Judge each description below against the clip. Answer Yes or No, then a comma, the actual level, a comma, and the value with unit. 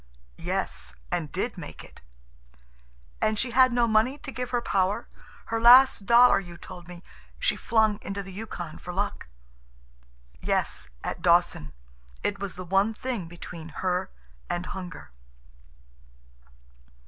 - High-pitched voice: Yes, high, 200 Hz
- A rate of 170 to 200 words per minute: No, slow, 135 wpm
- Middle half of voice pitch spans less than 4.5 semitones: No, average, 4.9 semitones